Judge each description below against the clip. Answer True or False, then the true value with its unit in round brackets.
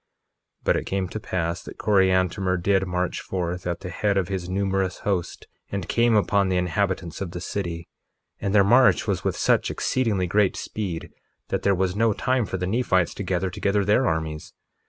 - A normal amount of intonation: False (2.1 semitones)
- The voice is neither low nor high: False (95 Hz)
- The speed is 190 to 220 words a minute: True (195 wpm)